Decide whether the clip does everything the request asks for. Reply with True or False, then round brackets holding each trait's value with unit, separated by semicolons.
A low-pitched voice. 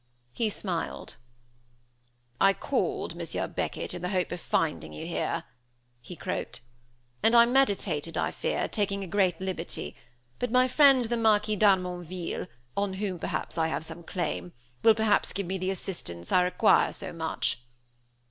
False (190 Hz)